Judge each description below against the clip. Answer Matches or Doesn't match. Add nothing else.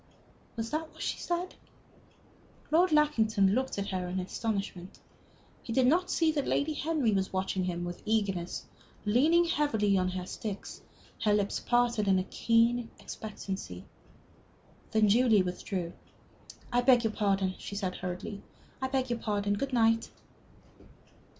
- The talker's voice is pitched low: Doesn't match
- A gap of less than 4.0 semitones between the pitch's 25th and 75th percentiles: Doesn't match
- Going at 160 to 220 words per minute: Doesn't match